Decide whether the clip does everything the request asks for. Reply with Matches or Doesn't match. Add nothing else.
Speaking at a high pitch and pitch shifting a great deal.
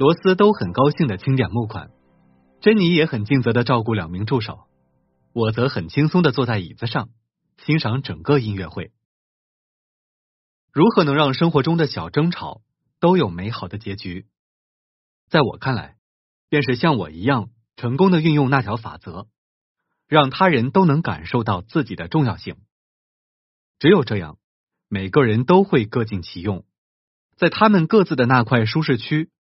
Doesn't match